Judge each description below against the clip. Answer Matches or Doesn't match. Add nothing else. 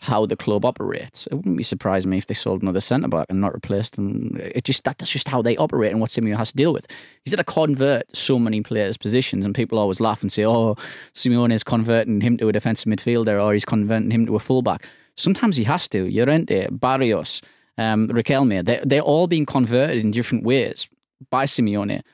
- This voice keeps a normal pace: Doesn't match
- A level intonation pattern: Doesn't match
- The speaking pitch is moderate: Doesn't match